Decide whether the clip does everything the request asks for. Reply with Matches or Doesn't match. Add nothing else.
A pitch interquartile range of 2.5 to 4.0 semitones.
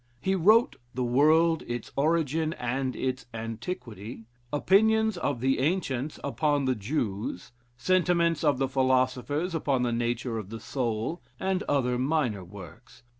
Doesn't match